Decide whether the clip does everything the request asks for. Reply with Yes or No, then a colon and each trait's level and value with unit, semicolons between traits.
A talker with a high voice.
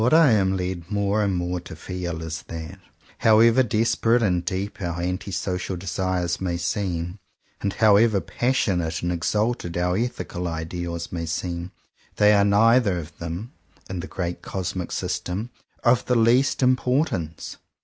No: very low, 95 Hz